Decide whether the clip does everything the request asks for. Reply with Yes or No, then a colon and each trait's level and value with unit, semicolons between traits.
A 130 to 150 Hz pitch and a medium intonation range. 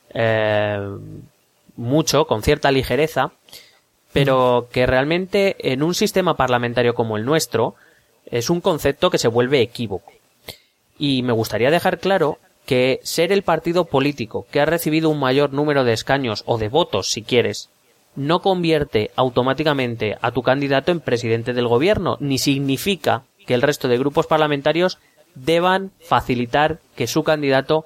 Yes: medium, 140 Hz; average, 4.5 semitones